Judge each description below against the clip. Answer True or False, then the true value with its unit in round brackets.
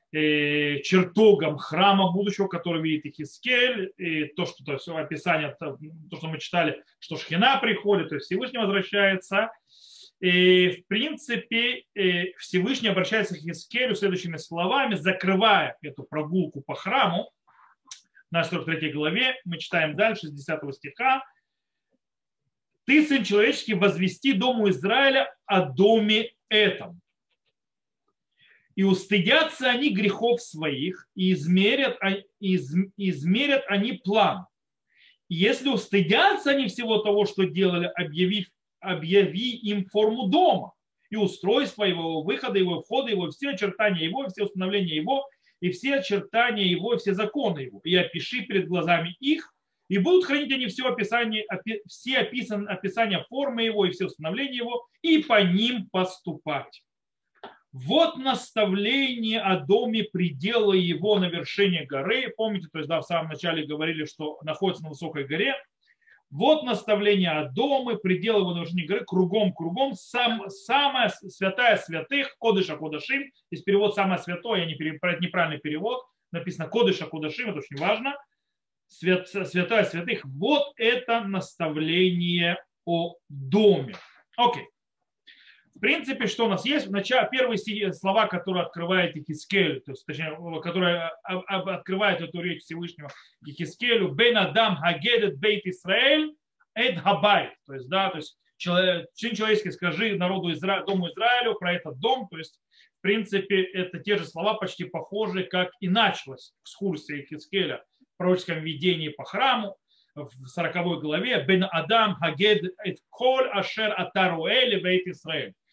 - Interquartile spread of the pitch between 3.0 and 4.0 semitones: False (4.6 semitones)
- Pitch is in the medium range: False (195 Hz)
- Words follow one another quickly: False (135 wpm)